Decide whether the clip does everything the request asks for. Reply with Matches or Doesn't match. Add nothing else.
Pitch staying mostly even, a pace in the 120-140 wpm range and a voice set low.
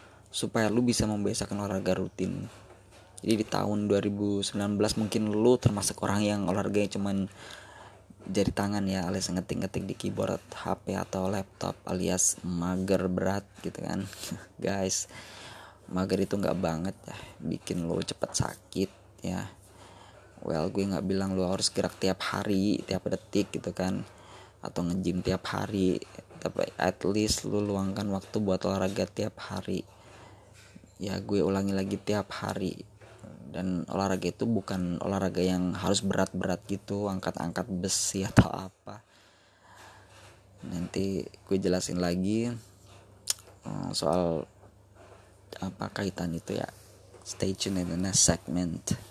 Matches